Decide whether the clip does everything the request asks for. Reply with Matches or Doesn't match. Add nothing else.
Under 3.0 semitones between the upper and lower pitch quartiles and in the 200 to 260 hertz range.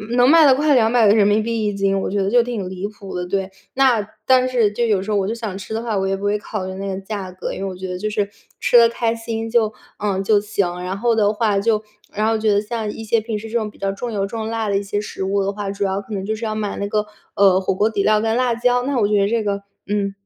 Matches